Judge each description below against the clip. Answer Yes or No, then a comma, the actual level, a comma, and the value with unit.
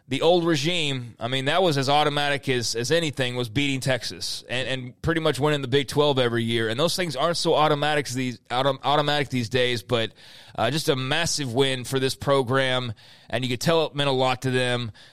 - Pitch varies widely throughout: No, average, 3.1 semitones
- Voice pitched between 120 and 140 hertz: Yes, low, 135 Hz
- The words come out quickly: Yes, fast, 210 wpm